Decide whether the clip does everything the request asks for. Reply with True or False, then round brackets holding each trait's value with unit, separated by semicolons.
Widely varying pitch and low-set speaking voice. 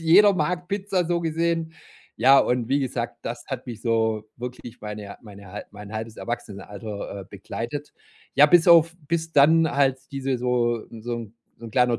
True (6.3 semitones; 125 Hz)